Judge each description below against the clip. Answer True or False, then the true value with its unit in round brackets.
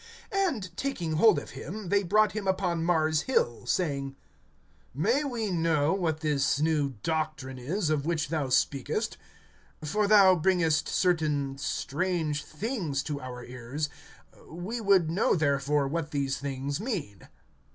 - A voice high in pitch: False (160 Hz)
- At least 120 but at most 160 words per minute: True (140 wpm)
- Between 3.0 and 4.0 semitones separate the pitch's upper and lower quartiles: False (5.0 semitones)